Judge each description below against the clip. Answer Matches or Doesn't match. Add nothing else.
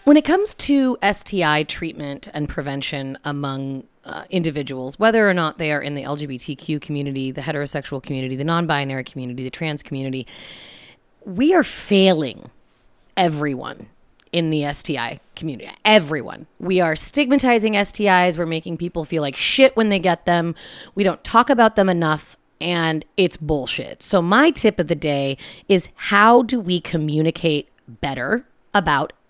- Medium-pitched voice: Matches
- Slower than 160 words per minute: Matches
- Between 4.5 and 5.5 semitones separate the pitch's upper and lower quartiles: Matches